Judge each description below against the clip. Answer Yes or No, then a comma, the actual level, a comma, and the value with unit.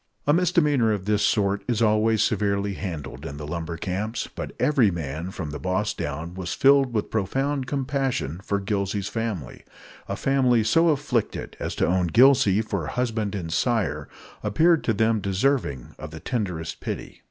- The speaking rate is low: No, average, 165 wpm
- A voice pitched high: No, low, 105 Hz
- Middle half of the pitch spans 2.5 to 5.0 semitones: No, wide, 5.5 semitones